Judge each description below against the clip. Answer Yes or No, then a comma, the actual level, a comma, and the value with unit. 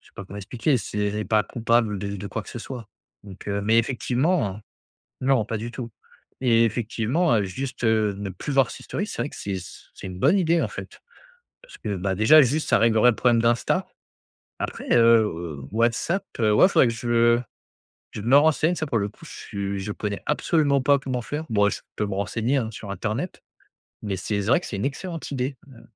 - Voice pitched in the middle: No, low, 115 Hz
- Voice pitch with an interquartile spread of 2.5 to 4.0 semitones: No, average, 4.6 semitones